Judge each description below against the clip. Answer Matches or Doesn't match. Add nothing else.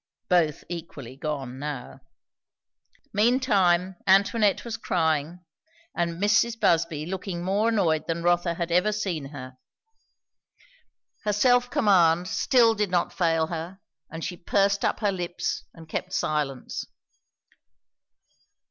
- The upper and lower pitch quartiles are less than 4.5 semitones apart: Matches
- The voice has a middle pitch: Matches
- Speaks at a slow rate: Matches